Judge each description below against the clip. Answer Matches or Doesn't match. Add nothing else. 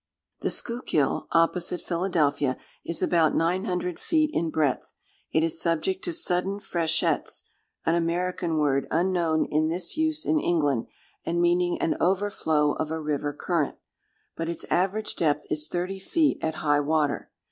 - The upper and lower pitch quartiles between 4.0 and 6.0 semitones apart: Doesn't match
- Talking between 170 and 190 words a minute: Doesn't match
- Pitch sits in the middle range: Matches